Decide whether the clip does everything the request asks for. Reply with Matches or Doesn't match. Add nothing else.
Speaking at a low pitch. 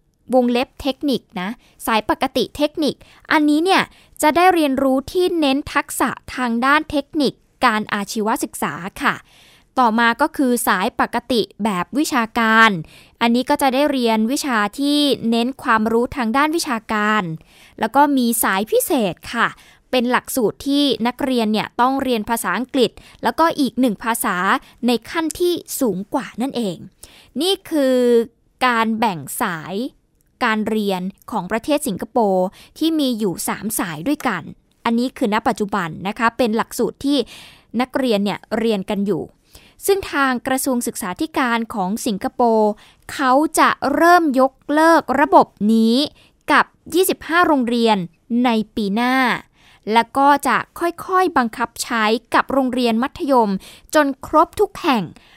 Doesn't match